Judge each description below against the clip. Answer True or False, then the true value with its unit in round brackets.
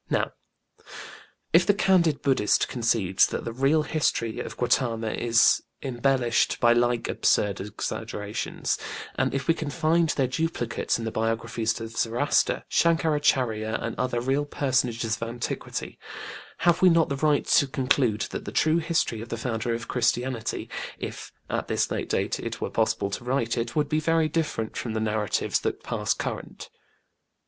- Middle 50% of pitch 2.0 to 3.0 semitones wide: False (4.8 semitones)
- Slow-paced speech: False (160 wpm)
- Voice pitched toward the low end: True (125 Hz)